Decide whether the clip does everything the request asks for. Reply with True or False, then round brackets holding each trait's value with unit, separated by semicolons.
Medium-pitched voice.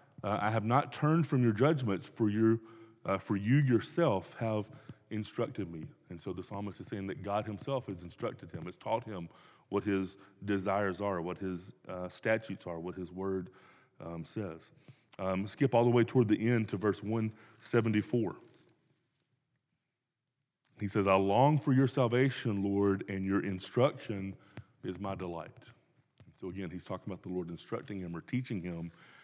False (105 Hz)